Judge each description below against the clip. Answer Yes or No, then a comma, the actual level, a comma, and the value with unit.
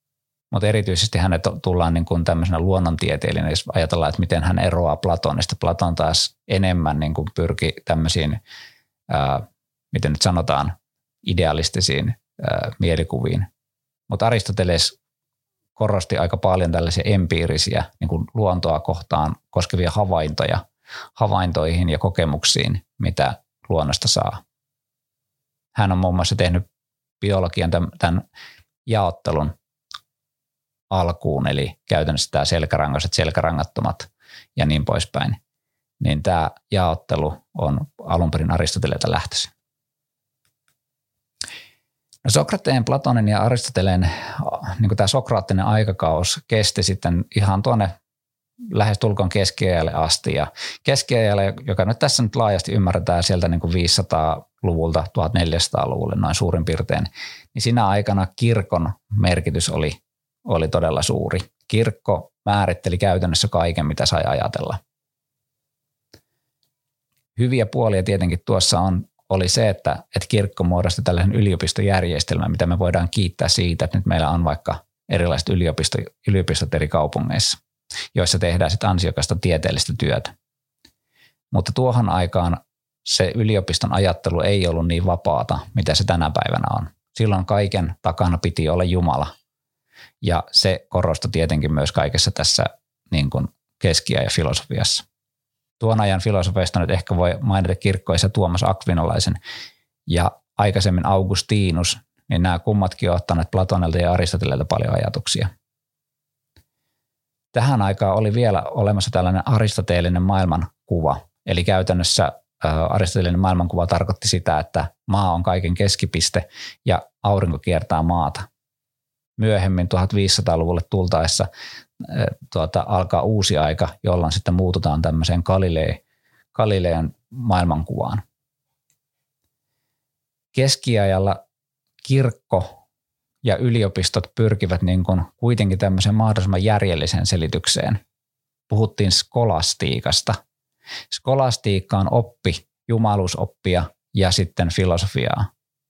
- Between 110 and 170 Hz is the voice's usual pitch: No, very low, 95 Hz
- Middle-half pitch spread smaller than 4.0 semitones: No, average, 4.7 semitones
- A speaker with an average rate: Yes, average, 110 wpm